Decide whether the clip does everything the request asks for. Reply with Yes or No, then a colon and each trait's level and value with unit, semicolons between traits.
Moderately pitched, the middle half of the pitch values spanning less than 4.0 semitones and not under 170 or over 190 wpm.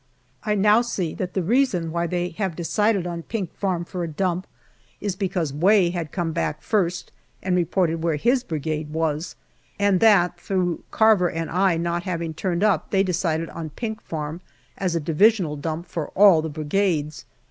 Yes: medium, 175 Hz; average, 3.1 semitones; average, 180 wpm